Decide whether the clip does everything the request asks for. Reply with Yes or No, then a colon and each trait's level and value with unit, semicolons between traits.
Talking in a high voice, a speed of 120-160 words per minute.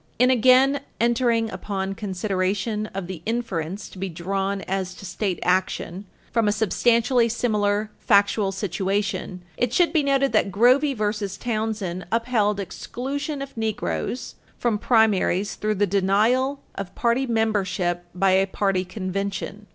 Yes: high, 210 Hz; slow, 135 wpm